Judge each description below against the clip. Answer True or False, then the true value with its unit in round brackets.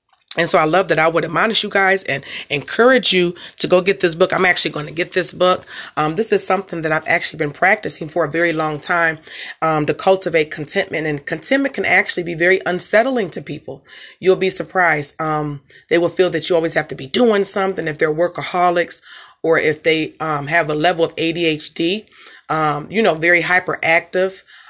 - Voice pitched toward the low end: False (170 Hz)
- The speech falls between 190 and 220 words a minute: True (205 wpm)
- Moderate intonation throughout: True (3.0 semitones)